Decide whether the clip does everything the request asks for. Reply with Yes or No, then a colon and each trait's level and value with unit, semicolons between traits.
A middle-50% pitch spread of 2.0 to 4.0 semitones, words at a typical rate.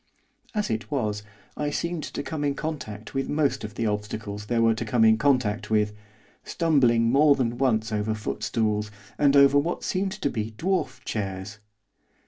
No: average, 4.9 semitones; average, 170 wpm